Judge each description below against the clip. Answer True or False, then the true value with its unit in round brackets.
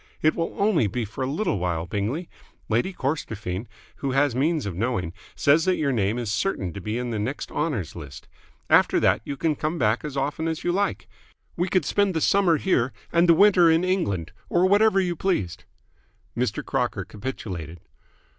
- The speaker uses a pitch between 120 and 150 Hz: True (140 Hz)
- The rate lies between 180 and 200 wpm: True (190 wpm)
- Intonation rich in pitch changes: True (8.4 semitones)